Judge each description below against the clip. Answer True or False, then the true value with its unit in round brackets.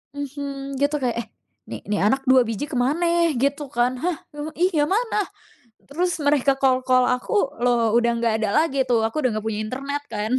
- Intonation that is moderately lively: True (3.4 semitones)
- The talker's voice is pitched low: False (270 Hz)